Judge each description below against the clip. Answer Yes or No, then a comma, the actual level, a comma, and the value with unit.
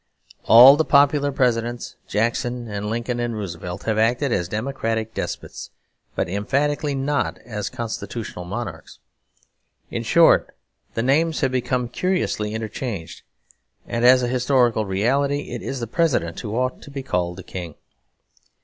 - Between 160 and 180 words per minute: No, average, 140 wpm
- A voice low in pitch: Yes, low, 120 Hz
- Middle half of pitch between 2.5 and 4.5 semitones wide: Yes, average, 4.2 semitones